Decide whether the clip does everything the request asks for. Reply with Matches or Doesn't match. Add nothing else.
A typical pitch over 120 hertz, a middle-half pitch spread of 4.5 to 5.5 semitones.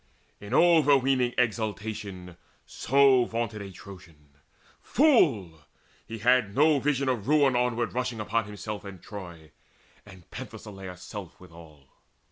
Doesn't match